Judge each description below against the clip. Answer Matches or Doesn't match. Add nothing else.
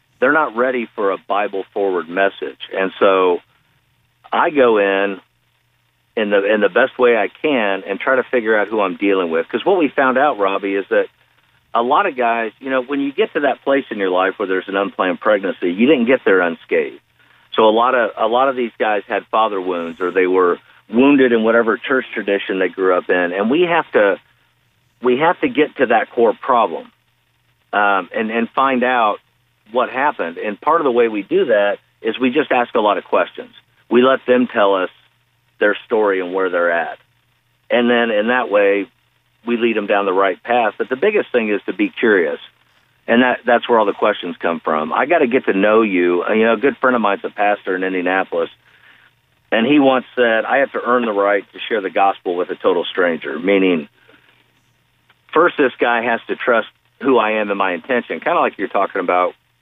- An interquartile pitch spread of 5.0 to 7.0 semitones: Matches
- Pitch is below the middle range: Matches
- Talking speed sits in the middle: Doesn't match